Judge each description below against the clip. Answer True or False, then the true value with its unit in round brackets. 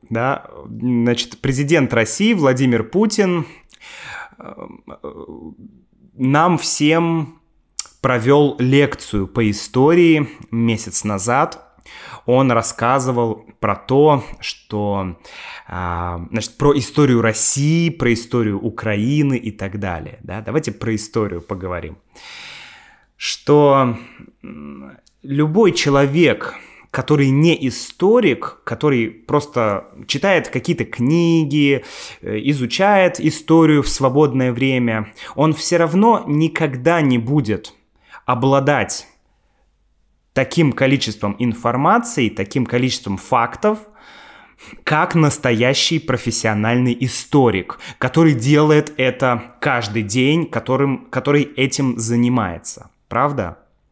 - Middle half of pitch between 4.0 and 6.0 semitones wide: True (4.8 semitones)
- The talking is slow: True (85 wpm)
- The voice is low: True (130 Hz)